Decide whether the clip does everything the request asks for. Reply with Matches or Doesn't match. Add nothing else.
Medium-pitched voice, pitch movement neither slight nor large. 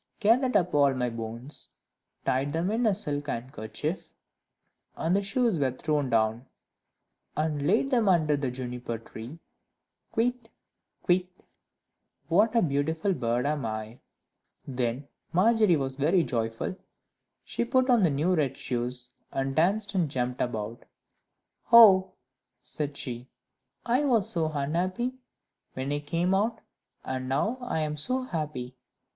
Doesn't match